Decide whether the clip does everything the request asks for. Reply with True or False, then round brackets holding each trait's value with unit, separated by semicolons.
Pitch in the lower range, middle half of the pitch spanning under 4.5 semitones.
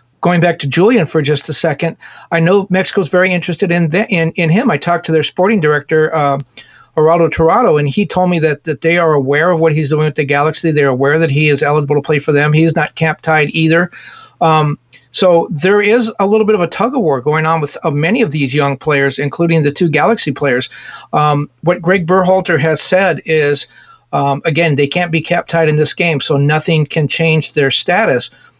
False (160 Hz; 2.8 semitones)